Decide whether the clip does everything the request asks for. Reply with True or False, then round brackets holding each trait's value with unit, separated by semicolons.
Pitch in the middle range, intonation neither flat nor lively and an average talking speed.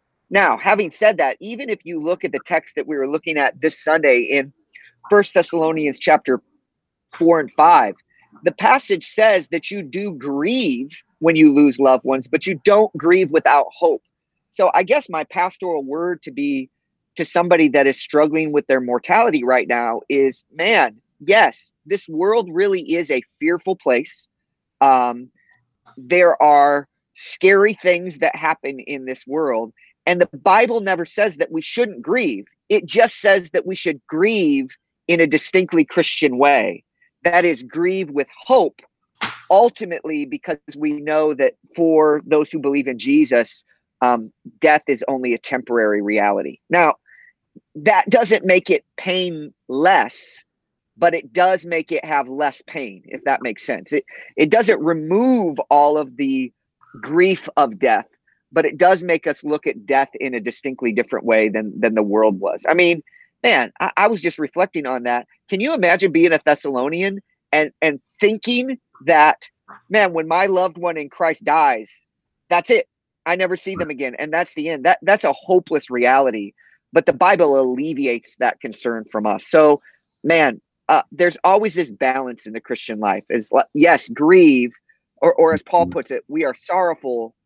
False (165 Hz; 6.5 semitones; 170 wpm)